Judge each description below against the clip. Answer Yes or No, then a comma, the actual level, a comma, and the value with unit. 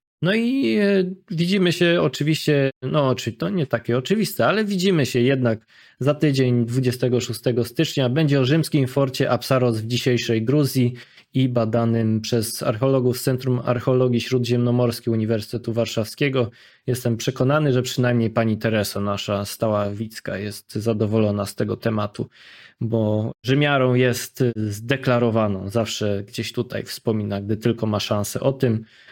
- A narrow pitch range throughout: No, average, 3.2 semitones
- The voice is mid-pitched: No, low, 120 Hz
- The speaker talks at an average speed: Yes, average, 135 wpm